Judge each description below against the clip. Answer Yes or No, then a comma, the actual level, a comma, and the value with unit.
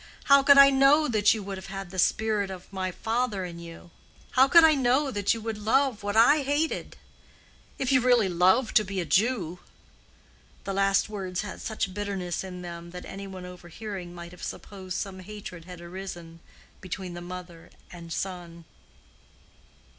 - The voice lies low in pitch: No, high, 195 Hz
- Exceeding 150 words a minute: Yes, average, 170 wpm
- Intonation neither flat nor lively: Yes, average, 4.0 semitones